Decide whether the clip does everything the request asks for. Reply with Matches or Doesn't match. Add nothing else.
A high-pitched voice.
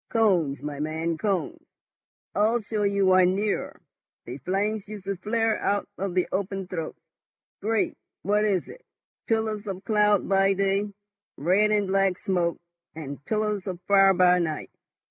Matches